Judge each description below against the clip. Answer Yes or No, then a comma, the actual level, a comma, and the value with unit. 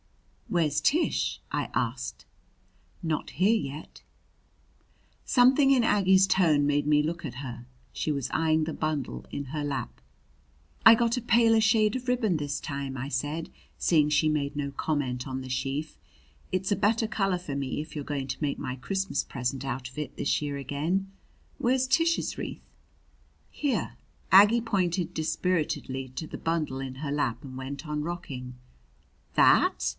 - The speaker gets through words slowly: No, average, 160 wpm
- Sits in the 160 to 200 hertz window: No, medium, 150 Hz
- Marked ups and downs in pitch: Yes, wide, 5.8 semitones